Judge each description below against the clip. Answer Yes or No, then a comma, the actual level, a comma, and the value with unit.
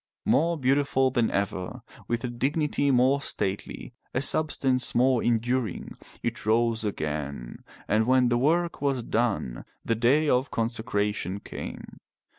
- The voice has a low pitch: Yes, low, 120 Hz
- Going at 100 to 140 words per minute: Yes, slow, 135 wpm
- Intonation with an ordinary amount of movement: Yes, average, 3.5 semitones